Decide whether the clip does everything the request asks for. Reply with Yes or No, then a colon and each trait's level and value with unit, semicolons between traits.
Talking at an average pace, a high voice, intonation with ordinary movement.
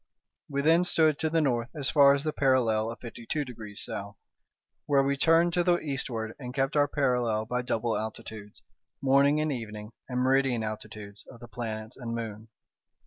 No: average, 185 wpm; low, 125 Hz; average, 4.2 semitones